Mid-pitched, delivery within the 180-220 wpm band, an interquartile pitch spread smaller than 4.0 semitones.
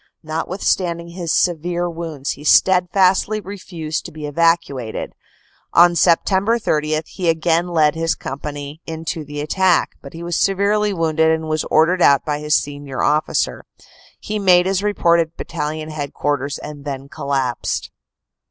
No: medium, 165 Hz; average, 145 wpm; average, 2.9 semitones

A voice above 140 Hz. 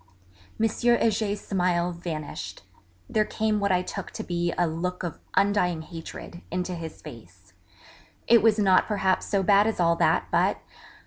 Yes: medium, 185 Hz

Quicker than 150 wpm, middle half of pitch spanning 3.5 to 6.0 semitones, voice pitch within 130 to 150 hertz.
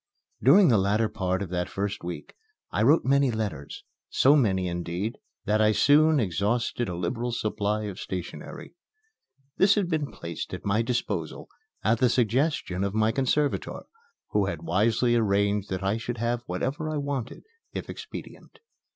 No: average, 160 wpm; average, 4.5 semitones; low, 110 Hz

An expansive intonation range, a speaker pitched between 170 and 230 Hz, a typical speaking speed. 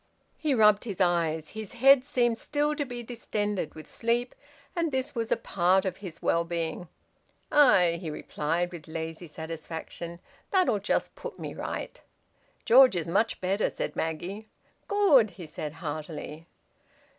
Yes: wide, 6.5 semitones; high, 190 Hz; average, 150 wpm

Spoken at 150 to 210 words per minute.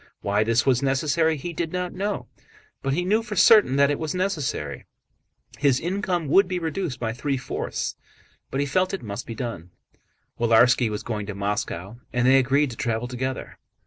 Yes: average, 185 wpm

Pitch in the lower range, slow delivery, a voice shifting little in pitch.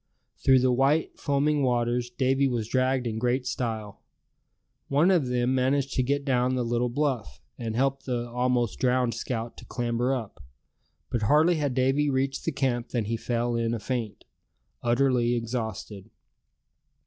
No: low, 125 Hz; average, 160 wpm; narrow, 2.2 semitones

